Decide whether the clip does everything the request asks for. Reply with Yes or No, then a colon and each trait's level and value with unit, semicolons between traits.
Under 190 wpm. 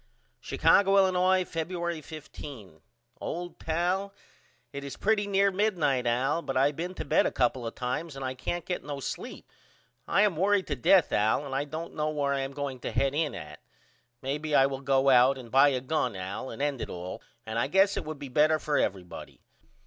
No: fast, 205 wpm